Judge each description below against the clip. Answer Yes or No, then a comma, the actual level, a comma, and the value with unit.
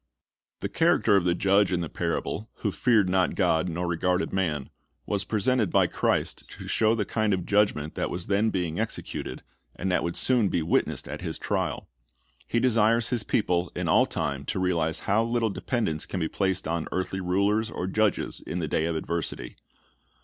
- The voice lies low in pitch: Yes, very low, 95 Hz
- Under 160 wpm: No, average, 190 wpm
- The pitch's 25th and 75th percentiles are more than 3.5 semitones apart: Yes, average, 4.0 semitones